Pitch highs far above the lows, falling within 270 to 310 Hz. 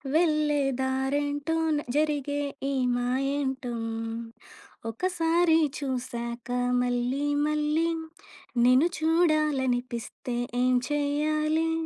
No: average, 3.3 semitones; very high, 290 Hz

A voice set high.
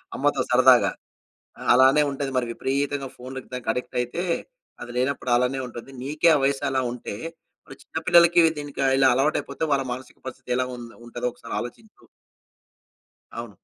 No: low, 130 Hz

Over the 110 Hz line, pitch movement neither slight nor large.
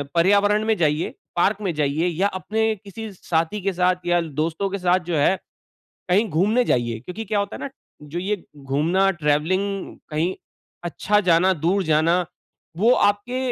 Yes: medium, 185 Hz; average, 3.9 semitones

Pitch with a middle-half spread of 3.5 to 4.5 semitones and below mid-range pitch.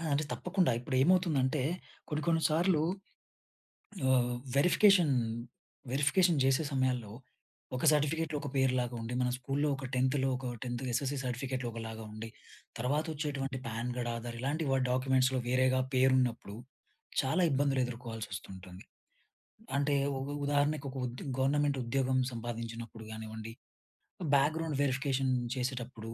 No: average, 3.1 semitones; low, 130 Hz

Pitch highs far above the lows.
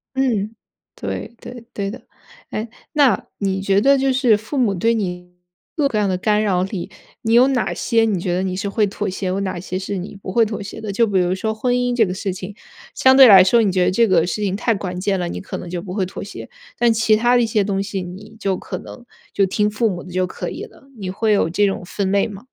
No: average, 3.3 semitones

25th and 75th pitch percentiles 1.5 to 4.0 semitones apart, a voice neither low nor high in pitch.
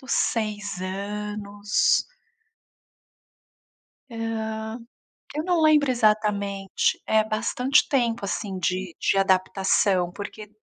No: narrow, 2.5 semitones; high, 210 Hz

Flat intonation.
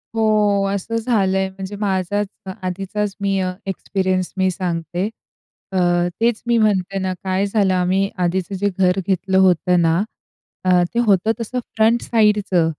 Yes: narrow, 2.1 semitones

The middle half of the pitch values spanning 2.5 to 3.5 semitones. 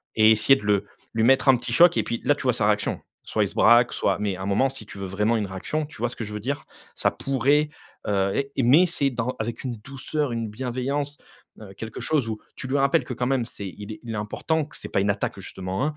No: average, 4.6 semitones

